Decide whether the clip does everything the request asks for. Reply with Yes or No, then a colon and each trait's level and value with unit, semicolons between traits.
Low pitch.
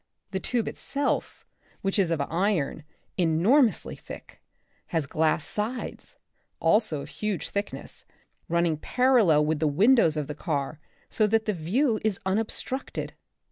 No: high, 190 Hz